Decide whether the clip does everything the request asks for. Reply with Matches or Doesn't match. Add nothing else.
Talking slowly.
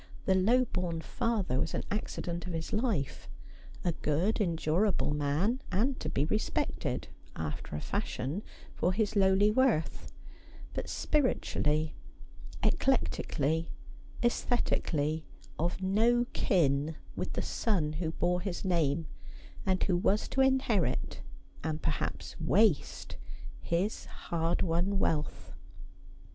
Matches